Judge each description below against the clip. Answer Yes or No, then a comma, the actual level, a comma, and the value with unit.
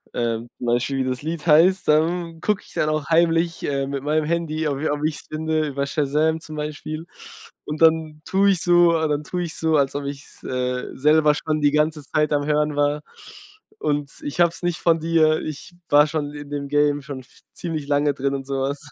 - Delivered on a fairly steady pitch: Yes, narrow, 2.0 semitones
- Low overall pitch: No, medium, 150 Hz